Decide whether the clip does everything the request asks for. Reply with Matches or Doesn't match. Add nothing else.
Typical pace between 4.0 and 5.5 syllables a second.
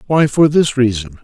Matches